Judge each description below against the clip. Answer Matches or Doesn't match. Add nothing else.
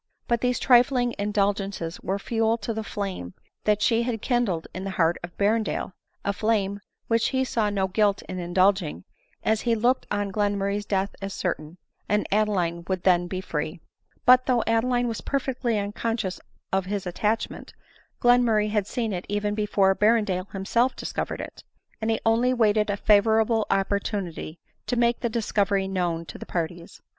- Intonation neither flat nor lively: Matches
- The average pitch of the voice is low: Doesn't match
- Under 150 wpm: Doesn't match